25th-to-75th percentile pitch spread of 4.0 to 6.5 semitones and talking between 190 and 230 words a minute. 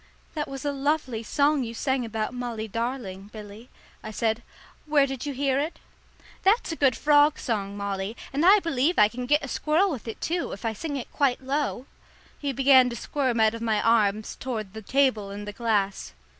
Yes: average, 4.6 semitones; average, 200 wpm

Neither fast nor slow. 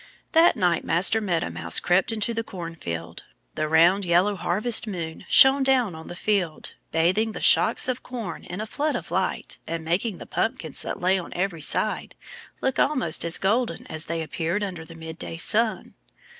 Yes: average, 180 wpm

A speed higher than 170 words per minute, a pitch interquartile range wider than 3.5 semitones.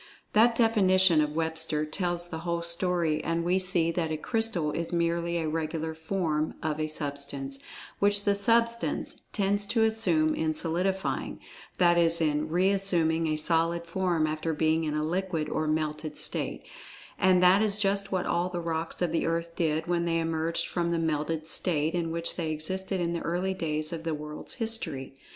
No: average, 180 wpm; average, 2.8 semitones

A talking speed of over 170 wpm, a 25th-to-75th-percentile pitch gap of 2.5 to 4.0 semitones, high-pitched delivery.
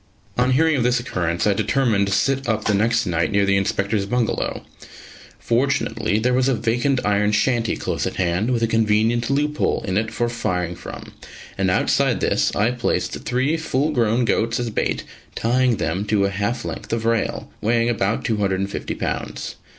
No: average, 180 wpm; average, 3.4 semitones; low, 115 Hz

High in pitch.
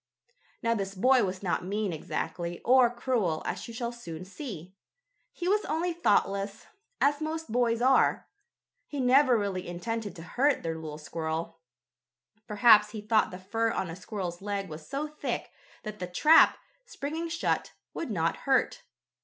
Yes: high, 210 Hz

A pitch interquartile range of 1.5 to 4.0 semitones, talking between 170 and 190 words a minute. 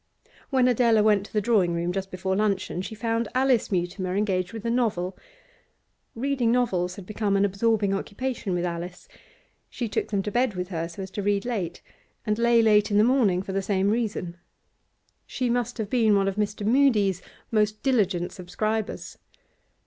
Yes: average, 3.3 semitones; average, 180 wpm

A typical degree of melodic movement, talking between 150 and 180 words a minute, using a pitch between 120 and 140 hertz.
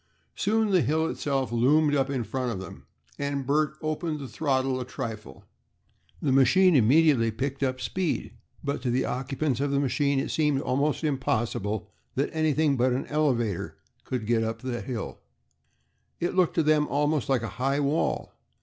Yes: average, 3.2 semitones; average, 170 wpm; low, 135 Hz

